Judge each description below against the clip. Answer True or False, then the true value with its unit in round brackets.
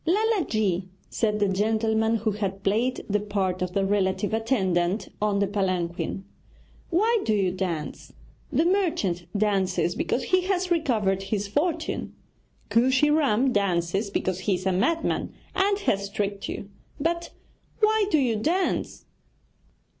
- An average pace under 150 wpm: True (140 wpm)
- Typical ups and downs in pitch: False (7.6 semitones)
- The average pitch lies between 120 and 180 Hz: False (210 Hz)